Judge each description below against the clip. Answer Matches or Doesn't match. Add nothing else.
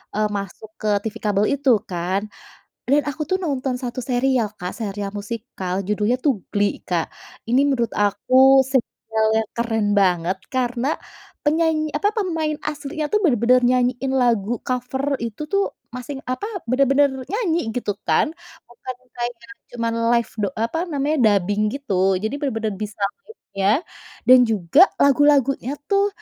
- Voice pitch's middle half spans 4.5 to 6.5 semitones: Matches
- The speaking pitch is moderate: Doesn't match